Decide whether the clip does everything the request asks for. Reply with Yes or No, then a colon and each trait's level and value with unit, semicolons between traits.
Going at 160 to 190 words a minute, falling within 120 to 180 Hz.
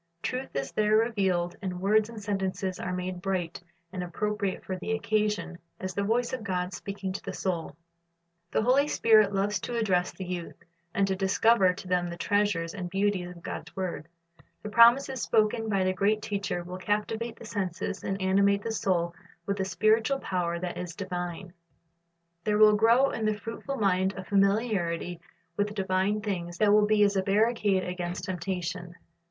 No: average, 180 wpm; high, 195 Hz